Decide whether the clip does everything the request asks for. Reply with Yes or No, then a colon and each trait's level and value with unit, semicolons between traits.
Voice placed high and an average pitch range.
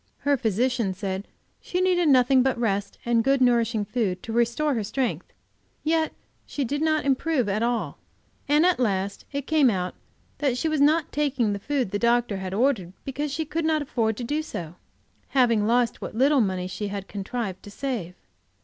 No: high, 245 Hz; wide, 5.7 semitones